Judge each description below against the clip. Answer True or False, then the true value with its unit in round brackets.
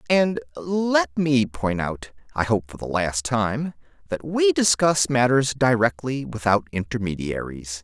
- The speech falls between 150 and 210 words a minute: False (140 wpm)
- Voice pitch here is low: True (125 Hz)